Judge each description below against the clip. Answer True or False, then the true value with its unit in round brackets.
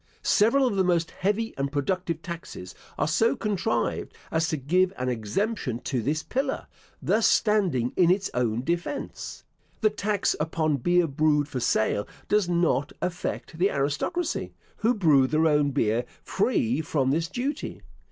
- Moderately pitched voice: True (165 Hz)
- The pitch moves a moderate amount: False (6.5 semitones)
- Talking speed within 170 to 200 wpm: False (150 wpm)